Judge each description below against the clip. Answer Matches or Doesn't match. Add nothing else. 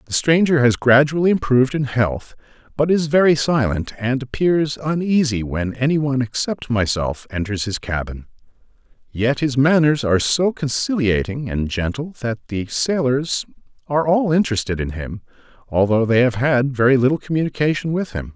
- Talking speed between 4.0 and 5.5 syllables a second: Matches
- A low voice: Matches